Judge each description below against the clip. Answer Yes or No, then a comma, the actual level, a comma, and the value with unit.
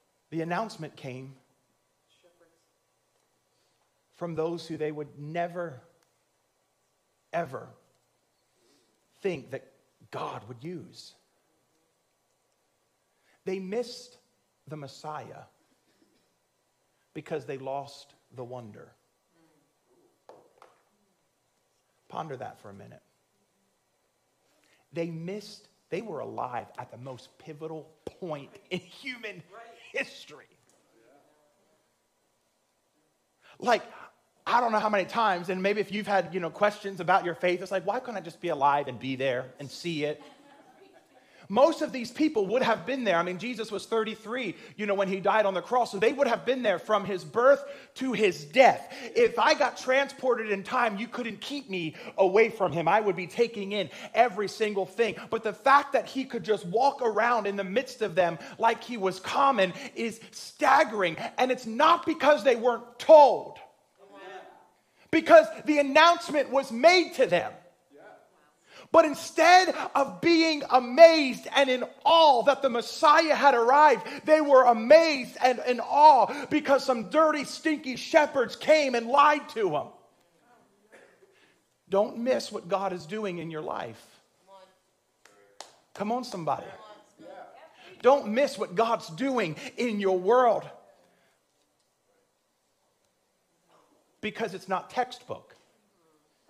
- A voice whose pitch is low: No, high, 220 Hz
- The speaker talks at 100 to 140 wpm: Yes, slow, 135 wpm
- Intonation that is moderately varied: No, wide, 6.8 semitones